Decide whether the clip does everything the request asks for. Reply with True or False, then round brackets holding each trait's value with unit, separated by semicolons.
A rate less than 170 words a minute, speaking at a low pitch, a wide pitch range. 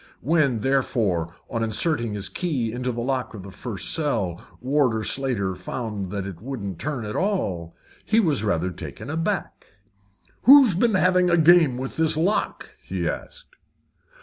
True (155 wpm; 125 Hz; 7.9 semitones)